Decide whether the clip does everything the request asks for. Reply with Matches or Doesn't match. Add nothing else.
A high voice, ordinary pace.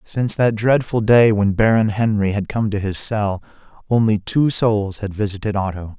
Doesn't match